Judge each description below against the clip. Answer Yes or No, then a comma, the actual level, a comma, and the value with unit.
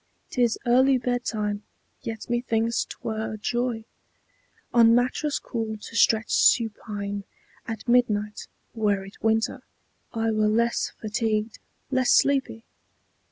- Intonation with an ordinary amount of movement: No, narrow, 2.0 semitones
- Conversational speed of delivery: No, slow, 115 wpm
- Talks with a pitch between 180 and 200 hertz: No, high, 225 Hz